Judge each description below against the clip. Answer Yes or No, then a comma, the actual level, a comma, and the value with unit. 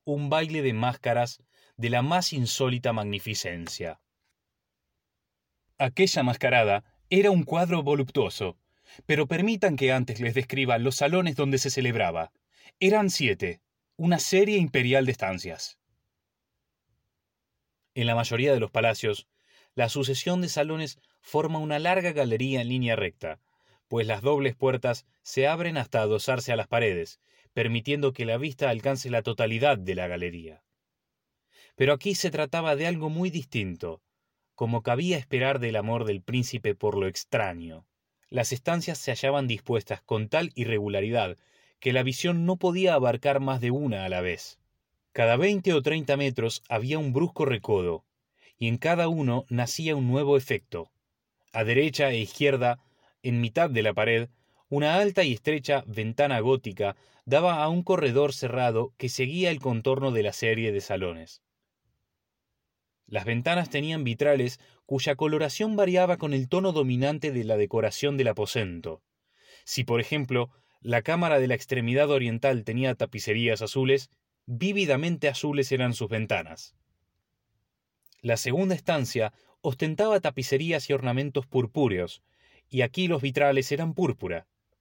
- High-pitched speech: No, low, 135 Hz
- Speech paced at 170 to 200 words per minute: No, average, 145 wpm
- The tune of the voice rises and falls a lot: No, average, 4.4 semitones